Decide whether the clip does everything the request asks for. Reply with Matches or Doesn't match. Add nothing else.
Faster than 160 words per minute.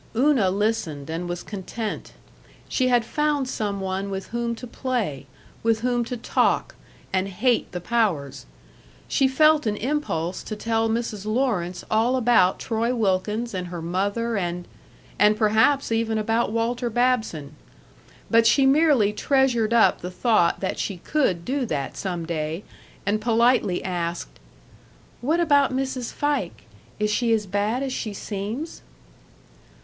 Doesn't match